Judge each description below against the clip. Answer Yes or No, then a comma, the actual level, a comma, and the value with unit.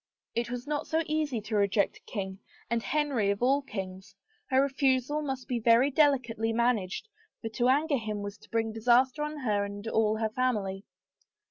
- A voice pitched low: No, high, 235 Hz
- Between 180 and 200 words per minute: Yes, average, 185 wpm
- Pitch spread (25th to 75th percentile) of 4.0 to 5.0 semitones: Yes, average, 4.3 semitones